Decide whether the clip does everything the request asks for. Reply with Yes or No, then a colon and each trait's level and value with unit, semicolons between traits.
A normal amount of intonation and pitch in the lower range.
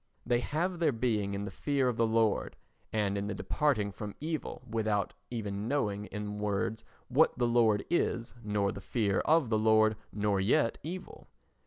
Yes: average, 3.6 semitones; low, 110 Hz